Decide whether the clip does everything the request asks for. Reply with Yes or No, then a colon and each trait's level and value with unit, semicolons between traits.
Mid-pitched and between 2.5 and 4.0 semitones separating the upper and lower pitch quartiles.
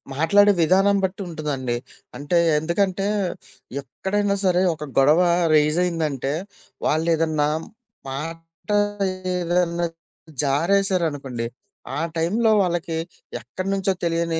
Yes: medium, 165 Hz; average, 3.6 semitones